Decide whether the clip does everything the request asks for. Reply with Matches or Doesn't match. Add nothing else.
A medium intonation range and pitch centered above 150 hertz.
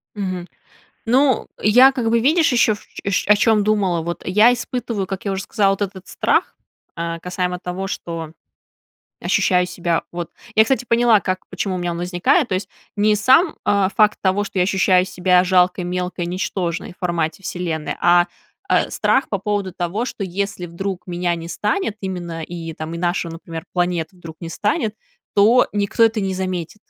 Matches